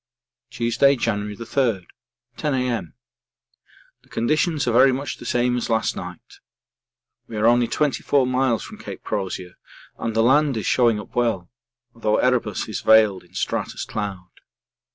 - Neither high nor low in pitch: No, low, 115 Hz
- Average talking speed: Yes, average, 150 wpm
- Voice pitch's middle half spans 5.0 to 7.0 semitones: No, average, 3.2 semitones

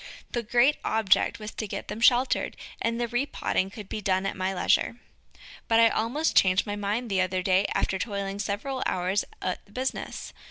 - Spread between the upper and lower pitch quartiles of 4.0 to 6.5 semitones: No, average, 3.5 semitones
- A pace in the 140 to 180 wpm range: No, average, 190 wpm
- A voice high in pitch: Yes, high, 210 Hz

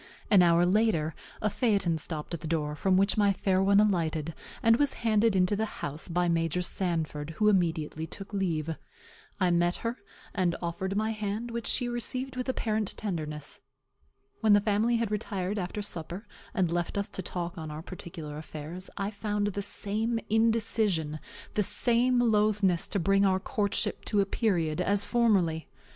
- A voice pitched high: Yes, high, 195 Hz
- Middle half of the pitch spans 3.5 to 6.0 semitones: Yes, average, 4.1 semitones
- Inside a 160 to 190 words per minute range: Yes, average, 170 wpm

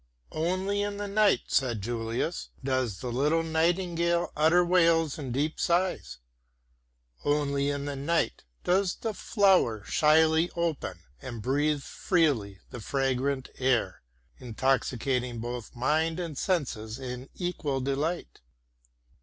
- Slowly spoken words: Yes, slow, 120 wpm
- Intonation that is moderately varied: Yes, average, 5.0 semitones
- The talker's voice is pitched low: No, medium, 145 Hz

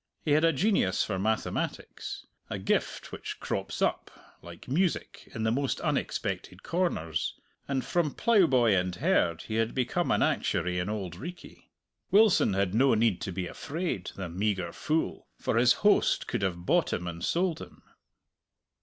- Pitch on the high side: No, low, 110 Hz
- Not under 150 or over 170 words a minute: Yes, average, 165 wpm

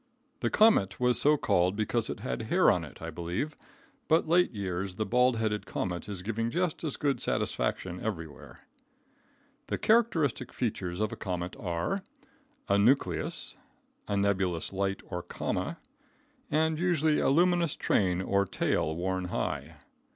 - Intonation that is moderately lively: No, wide, 8.5 semitones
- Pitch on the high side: No, low, 105 Hz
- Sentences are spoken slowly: No, average, 150 wpm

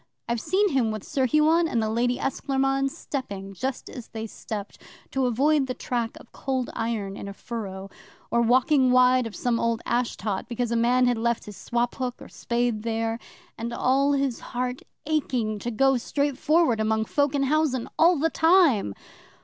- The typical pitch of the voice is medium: No, high, 245 Hz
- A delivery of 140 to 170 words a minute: No, average, 180 wpm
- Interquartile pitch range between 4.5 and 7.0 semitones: No, average, 3.1 semitones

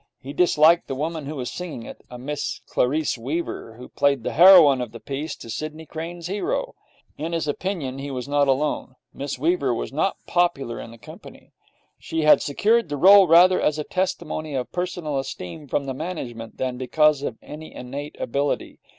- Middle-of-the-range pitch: Yes, medium, 150 Hz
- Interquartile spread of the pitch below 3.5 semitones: No, average, 4.1 semitones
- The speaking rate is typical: Yes, average, 185 wpm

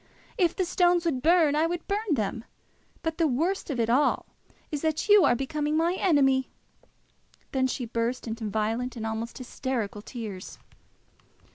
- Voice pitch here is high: Yes, very high, 270 Hz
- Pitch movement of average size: No, wide, 6.0 semitones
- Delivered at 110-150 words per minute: No, average, 160 wpm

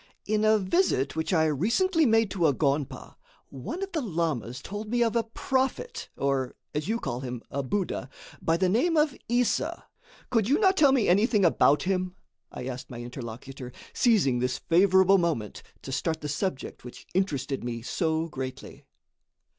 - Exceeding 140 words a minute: Yes, average, 170 wpm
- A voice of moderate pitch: Yes, medium, 175 Hz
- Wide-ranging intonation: Yes, wide, 8.8 semitones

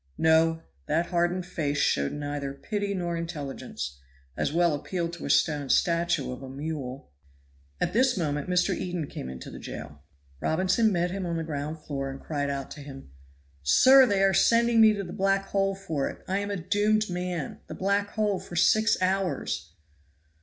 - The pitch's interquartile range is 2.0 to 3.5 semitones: No, average, 5.2 semitones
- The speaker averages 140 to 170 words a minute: No, average, 180 wpm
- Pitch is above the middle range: No, medium, 170 Hz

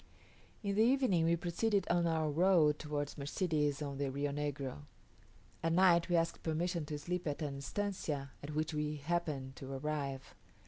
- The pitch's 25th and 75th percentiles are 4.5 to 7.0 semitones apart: No, average, 3.2 semitones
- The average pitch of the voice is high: No, medium, 155 Hz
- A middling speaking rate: Yes, average, 170 wpm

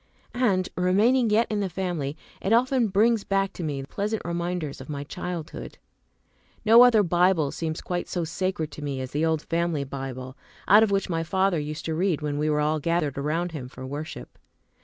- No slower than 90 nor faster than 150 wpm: No, average, 195 wpm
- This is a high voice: No, medium, 170 Hz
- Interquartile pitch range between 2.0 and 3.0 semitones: No, average, 4.6 semitones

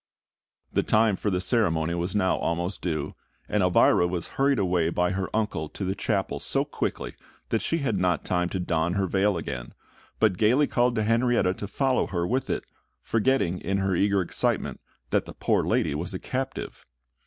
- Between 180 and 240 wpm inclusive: Yes, average, 190 wpm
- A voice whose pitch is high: No, very low, 95 Hz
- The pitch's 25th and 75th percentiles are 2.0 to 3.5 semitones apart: No, average, 3.9 semitones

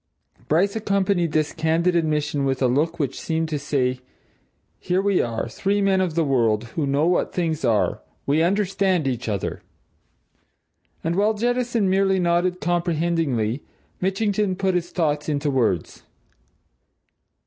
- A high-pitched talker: No, medium, 165 Hz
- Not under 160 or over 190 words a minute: No, average, 140 wpm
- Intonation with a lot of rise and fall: No, average, 4.9 semitones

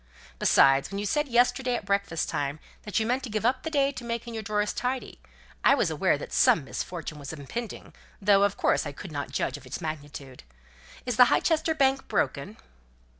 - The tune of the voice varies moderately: No, wide, 8.4 semitones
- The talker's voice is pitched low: No, high, 210 Hz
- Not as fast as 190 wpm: No, average, 200 wpm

